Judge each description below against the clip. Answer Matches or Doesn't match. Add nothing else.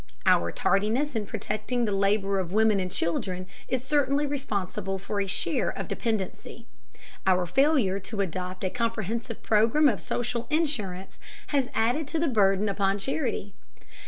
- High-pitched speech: Matches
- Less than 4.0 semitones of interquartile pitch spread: Doesn't match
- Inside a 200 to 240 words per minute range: Doesn't match